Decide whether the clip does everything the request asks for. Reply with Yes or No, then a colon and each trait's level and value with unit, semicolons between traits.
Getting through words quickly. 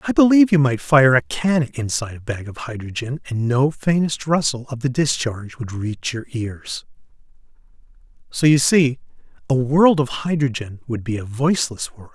No: average, 175 wpm